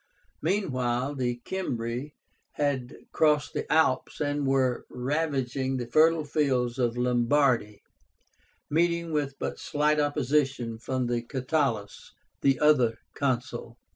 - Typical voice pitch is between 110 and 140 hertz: Yes, low, 135 Hz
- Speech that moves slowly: Yes, slow, 105 wpm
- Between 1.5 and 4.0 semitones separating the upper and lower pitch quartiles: Yes, average, 3.5 semitones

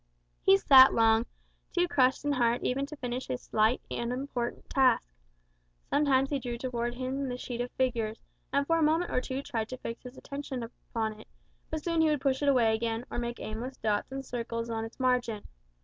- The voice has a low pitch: No, very high, 250 Hz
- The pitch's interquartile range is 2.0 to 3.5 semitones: Yes, average, 2.8 semitones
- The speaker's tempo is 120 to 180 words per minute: No, average, 200 wpm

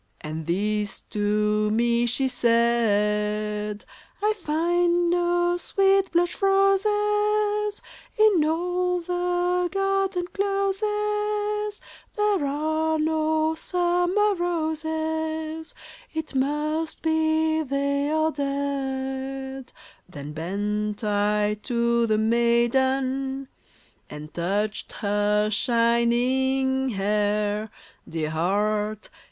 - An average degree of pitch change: No, wide, 8.7 semitones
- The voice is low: No, very high, 280 Hz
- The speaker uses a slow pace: Yes, slow, 90 wpm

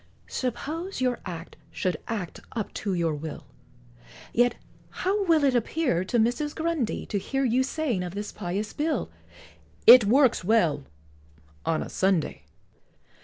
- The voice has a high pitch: Yes, high, 230 Hz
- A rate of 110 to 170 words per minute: Yes, average, 140 wpm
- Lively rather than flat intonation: Yes, wide, 7.2 semitones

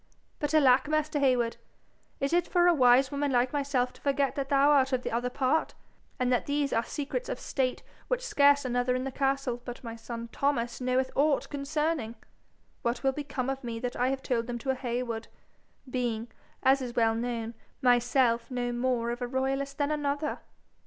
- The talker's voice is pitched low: No, very high, 260 Hz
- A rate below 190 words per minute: No, average, 195 wpm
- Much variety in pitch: No, narrow, 2.6 semitones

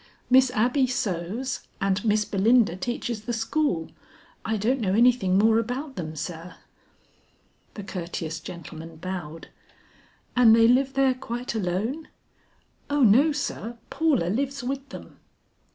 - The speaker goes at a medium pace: No, slow, 130 wpm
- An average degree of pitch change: No, wide, 5.7 semitones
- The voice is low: No, high, 225 Hz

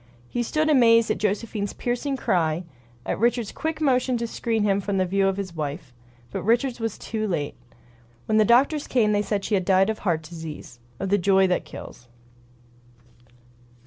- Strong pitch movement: No, average, 4.0 semitones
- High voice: Yes, high, 205 Hz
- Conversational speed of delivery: Yes, average, 185 wpm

